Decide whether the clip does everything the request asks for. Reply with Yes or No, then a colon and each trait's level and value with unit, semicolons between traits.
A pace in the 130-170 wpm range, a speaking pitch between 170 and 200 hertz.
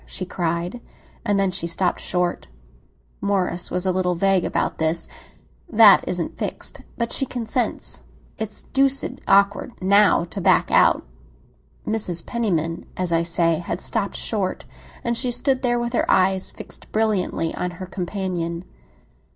Yes: average, 145 wpm; high, 190 Hz